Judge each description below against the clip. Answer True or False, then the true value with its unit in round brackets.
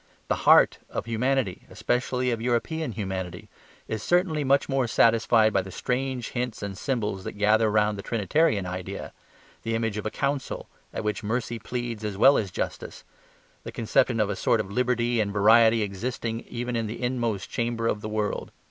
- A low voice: True (115 Hz)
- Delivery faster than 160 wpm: True (180 wpm)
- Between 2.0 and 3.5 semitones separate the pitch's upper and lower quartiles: True (2.9 semitones)